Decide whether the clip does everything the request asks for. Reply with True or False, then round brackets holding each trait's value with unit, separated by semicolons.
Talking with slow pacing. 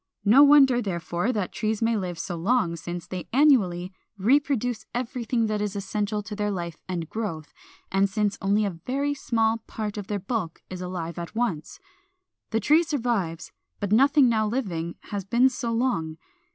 False (170 wpm)